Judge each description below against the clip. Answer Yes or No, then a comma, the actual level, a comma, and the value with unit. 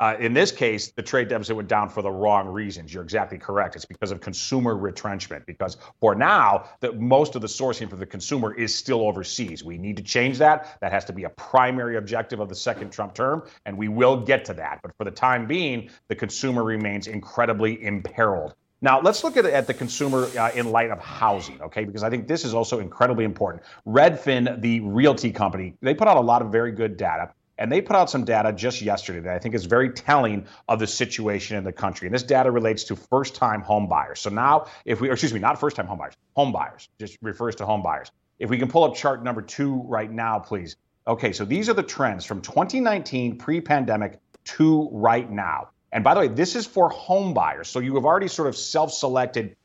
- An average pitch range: Yes, average, 3.9 semitones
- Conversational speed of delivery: No, fast, 230 wpm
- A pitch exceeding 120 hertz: No, low, 115 Hz